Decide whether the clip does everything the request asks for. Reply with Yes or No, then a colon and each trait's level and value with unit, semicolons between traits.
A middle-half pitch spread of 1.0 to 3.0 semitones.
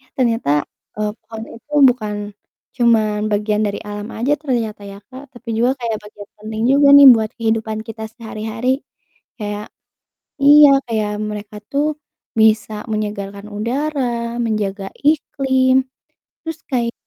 No: average, 3.4 semitones